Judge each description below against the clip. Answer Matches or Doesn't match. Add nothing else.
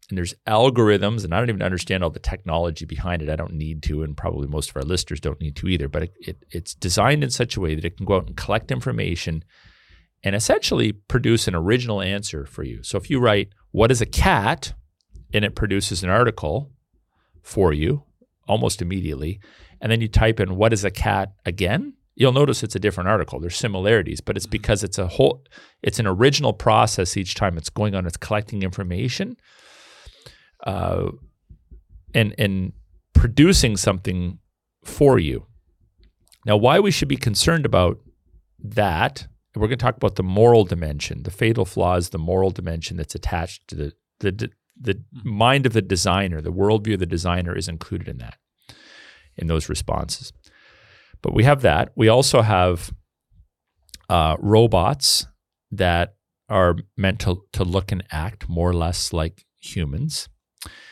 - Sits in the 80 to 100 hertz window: Matches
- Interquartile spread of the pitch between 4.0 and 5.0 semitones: Matches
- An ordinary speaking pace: Matches